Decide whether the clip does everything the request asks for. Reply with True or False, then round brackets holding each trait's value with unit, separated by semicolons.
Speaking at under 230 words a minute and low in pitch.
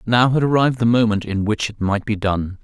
False (250 wpm; 110 Hz)